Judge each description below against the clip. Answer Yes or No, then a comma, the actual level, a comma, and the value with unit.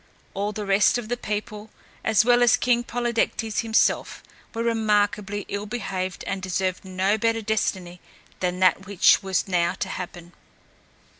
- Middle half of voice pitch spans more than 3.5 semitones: No, average, 3.0 semitones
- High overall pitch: Yes, high, 205 Hz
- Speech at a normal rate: Yes, average, 150 wpm